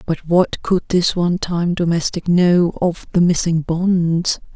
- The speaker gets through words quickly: No, average, 145 wpm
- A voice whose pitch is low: No, medium, 175 Hz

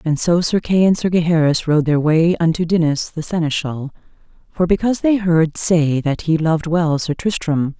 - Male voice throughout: No, female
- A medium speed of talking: Yes, average, 195 wpm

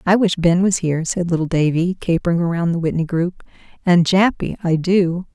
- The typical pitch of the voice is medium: Yes, medium, 175 Hz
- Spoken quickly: No, average, 190 wpm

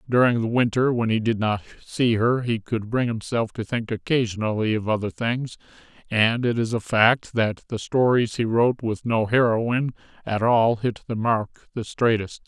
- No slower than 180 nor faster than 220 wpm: Yes, average, 190 wpm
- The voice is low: Yes, low, 115 Hz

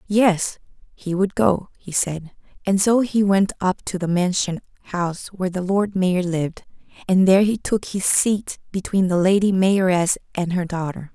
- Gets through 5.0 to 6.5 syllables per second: No, 4.6 syllables/s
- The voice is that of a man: No, female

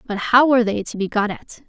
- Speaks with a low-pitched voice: No, high, 225 Hz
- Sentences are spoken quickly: Yes, fast, 285 wpm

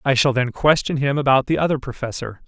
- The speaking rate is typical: No, fast, 220 wpm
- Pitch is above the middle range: No, low, 130 Hz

